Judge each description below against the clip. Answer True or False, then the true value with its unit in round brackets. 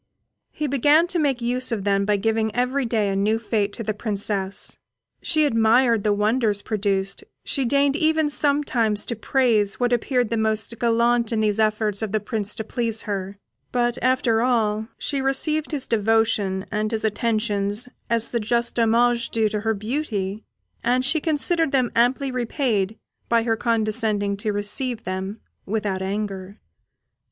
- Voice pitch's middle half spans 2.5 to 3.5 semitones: True (3.1 semitones)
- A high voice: True (225 Hz)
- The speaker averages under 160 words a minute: False (165 wpm)